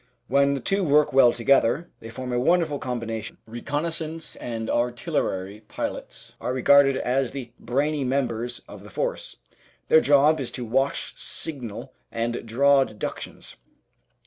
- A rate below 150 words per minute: Yes, average, 140 wpm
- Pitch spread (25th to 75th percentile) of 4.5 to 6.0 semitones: No, average, 3.3 semitones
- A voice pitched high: No, low, 130 Hz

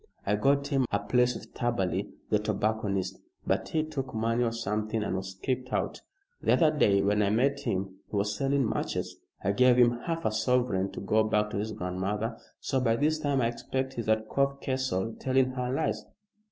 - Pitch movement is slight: No, average, 4.2 semitones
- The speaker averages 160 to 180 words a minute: No, average, 200 wpm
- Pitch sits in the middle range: No, low, 115 Hz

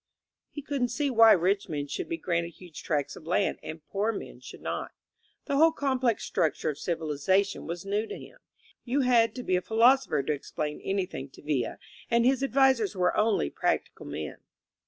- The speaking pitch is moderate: No, high, 200 Hz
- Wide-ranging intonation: Yes, wide, 7.3 semitones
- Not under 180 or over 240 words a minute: Yes, average, 195 wpm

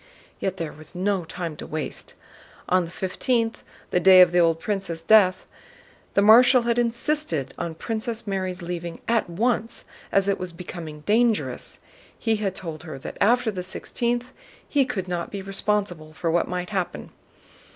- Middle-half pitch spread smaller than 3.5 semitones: No, average, 4.5 semitones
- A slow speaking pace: No, average, 165 wpm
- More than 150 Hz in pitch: Yes, high, 190 Hz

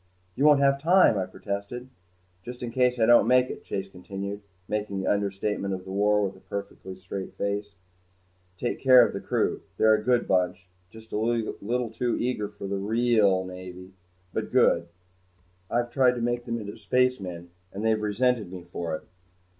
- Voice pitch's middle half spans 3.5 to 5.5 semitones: Yes, average, 3.9 semitones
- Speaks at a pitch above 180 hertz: No, low, 105 Hz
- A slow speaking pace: No, average, 180 wpm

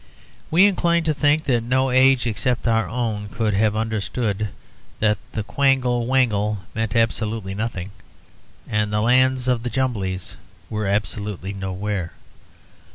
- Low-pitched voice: Yes, low, 115 Hz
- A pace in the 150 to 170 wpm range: No, slow, 135 wpm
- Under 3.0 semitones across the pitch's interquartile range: No, average, 3.6 semitones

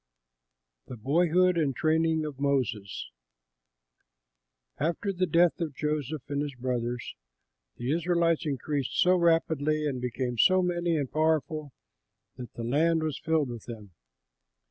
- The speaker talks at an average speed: No, slow, 130 wpm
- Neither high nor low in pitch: Yes, medium, 150 Hz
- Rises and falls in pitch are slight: No, average, 4.3 semitones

